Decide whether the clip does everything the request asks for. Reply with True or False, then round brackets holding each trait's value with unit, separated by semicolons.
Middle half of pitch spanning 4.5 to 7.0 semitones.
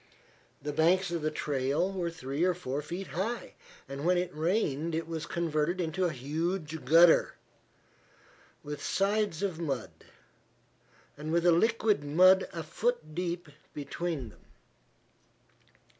False (3.3 semitones)